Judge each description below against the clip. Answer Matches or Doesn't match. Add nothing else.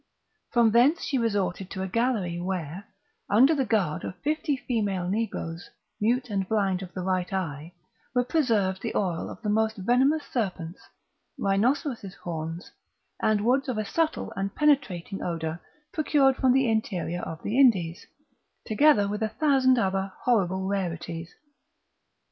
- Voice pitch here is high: Matches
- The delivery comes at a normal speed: Matches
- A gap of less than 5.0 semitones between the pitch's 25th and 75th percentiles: Doesn't match